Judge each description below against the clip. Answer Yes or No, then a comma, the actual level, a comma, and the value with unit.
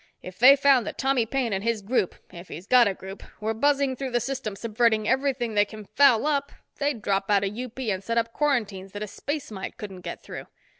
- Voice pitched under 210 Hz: No, high, 230 Hz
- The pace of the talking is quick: Yes, fast, 230 wpm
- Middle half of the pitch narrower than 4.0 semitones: No, average, 4.6 semitones